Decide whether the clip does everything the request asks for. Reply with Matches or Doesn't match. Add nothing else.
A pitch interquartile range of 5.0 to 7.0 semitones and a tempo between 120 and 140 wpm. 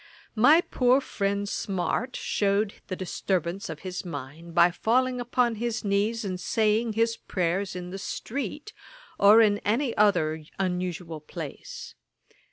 Doesn't match